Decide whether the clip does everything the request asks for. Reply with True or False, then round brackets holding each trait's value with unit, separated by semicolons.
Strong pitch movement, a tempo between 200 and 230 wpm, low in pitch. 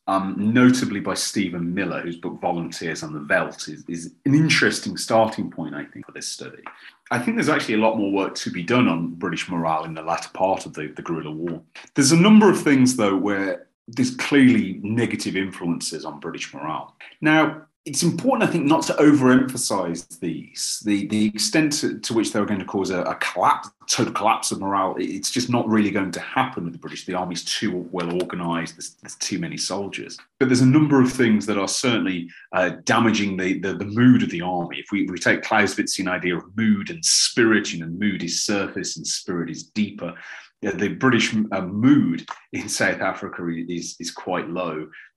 True (6.5 semitones; 205 wpm; 100 Hz)